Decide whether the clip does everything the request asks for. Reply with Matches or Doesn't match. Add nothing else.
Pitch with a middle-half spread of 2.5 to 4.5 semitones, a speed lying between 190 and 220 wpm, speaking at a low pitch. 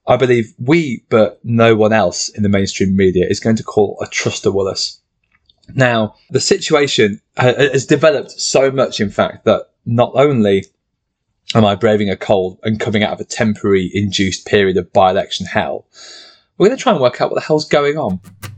Doesn't match